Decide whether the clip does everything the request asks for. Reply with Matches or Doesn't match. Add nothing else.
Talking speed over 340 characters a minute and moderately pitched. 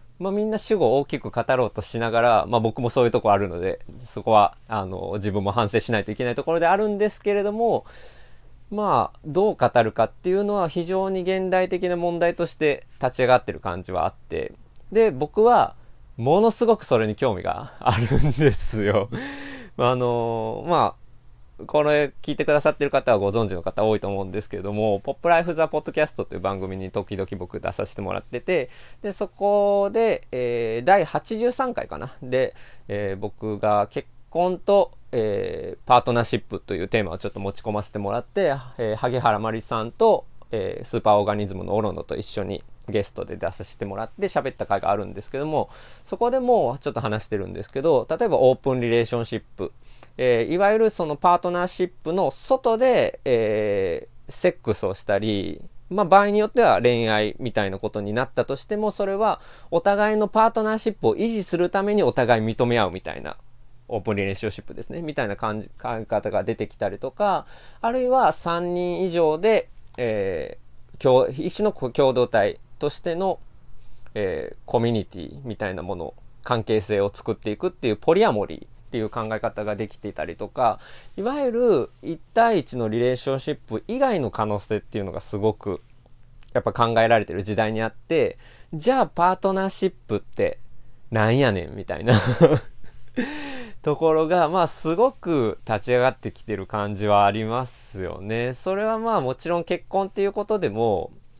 Doesn't match